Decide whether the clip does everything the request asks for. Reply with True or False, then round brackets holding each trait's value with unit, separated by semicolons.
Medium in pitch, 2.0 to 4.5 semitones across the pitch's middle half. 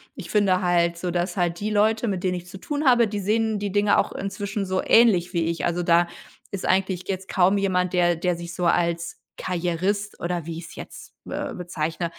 True (180 Hz; 2.7 semitones)